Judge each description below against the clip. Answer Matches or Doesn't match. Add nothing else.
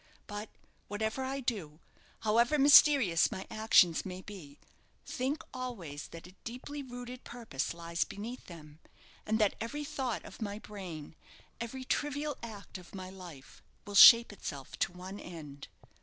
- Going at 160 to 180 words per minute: Doesn't match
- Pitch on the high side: Matches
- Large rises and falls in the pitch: Matches